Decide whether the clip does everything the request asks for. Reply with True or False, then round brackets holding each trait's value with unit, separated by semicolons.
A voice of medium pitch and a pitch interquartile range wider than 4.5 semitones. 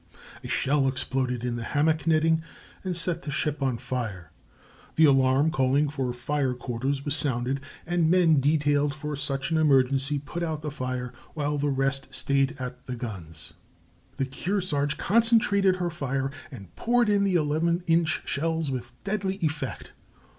False (145 Hz; 3.7 semitones)